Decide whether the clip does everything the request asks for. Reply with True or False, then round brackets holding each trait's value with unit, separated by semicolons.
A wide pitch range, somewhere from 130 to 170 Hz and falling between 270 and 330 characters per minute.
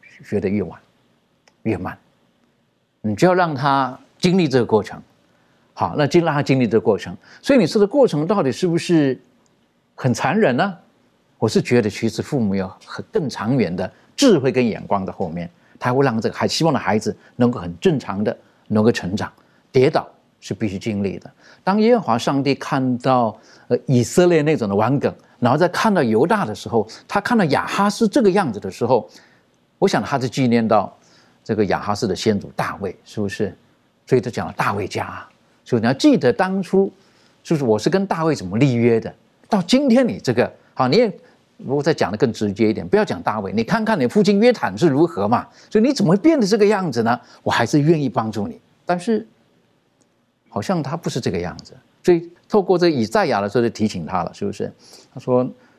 True (8.8 semitones; 140 Hz; 295 characters per minute)